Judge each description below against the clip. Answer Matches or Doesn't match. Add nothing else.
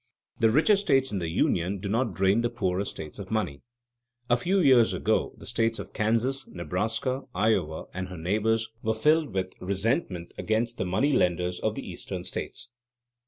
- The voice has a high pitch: Doesn't match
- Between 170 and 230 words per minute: Matches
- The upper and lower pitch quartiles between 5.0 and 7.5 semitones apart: Doesn't match